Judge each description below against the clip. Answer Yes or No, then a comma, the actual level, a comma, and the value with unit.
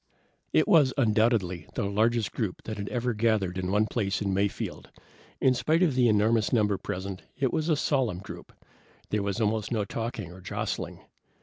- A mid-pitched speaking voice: No, low, 110 Hz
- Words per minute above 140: Yes, average, 180 wpm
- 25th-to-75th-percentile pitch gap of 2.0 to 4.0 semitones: Yes, average, 3.5 semitones